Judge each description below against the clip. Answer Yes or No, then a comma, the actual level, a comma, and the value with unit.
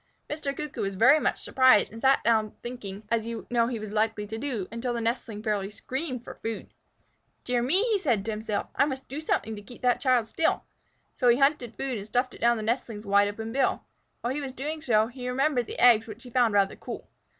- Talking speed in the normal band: No, fast, 230 wpm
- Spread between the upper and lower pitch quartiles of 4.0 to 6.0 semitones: No, average, 3.2 semitones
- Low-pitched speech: No, high, 235 Hz